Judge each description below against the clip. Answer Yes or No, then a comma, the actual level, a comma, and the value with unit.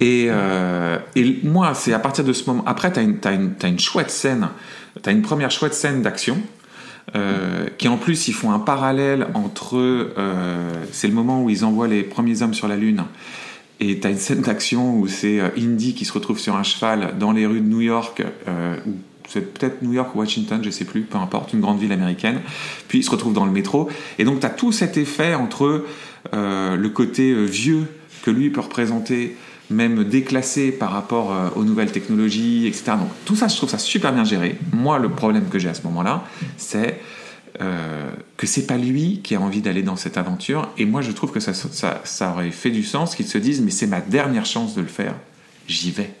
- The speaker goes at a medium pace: No, fast, 225 wpm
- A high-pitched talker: No, low, 130 Hz